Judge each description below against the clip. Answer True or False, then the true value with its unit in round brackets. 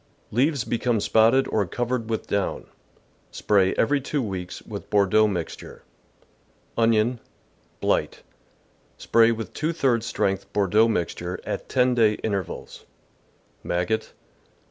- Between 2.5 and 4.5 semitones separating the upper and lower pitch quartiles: True (3.2 semitones)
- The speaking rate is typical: False (125 wpm)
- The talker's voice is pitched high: False (110 Hz)